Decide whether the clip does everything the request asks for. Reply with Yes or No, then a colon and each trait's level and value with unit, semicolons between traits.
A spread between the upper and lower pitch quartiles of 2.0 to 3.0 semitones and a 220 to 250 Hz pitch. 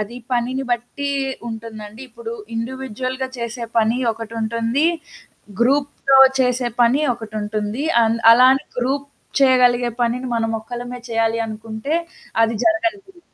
Yes: narrow, 2.6 semitones; high, 240 Hz